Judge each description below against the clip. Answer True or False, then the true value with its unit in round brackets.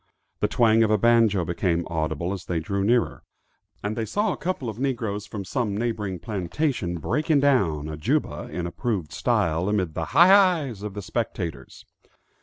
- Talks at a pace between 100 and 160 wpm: False (175 wpm)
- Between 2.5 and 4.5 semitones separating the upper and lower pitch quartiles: False (5.5 semitones)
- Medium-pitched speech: False (105 Hz)